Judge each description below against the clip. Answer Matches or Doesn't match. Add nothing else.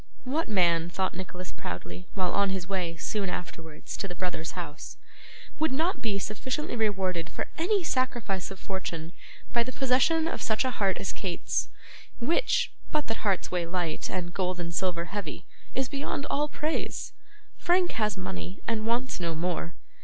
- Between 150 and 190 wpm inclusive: Matches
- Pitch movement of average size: Doesn't match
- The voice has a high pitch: Matches